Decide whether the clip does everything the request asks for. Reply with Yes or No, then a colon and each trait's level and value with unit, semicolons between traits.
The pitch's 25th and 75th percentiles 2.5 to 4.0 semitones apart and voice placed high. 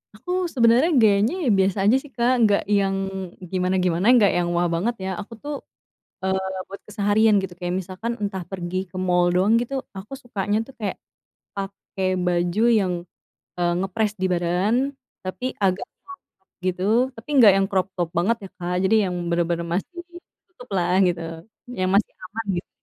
Yes: average, 3.3 semitones; high, 195 Hz